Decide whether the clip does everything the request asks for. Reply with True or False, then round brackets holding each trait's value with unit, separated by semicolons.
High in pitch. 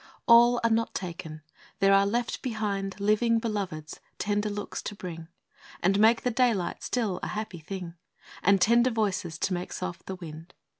True (200 Hz)